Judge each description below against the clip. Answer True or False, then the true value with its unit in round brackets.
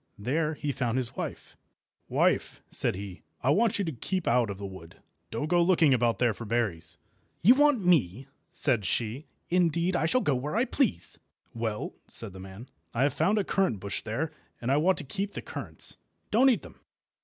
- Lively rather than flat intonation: True (8.2 semitones)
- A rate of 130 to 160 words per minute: False (200 wpm)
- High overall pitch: False (135 Hz)